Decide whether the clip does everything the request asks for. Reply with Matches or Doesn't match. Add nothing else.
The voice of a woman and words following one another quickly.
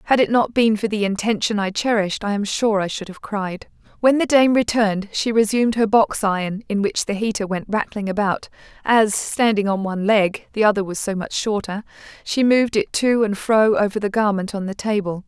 Matches